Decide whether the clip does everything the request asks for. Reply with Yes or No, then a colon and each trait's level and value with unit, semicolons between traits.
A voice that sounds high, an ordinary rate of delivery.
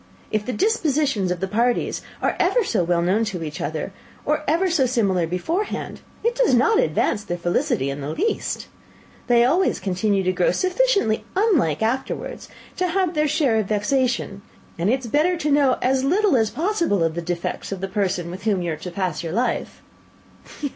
Yes: high, 230 Hz; average, 190 wpm